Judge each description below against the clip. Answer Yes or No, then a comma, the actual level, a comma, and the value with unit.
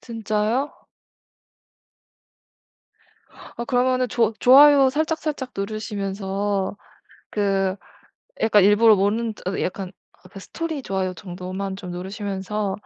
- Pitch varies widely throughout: No, average, 3.8 semitones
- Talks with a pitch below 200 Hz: No, high, 205 Hz